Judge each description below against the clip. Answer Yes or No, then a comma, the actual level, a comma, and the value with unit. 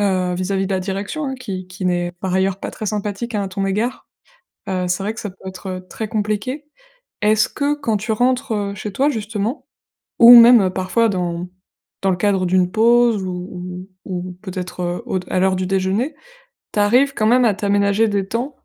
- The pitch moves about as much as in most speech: Yes, average, 3.4 semitones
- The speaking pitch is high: Yes, high, 200 Hz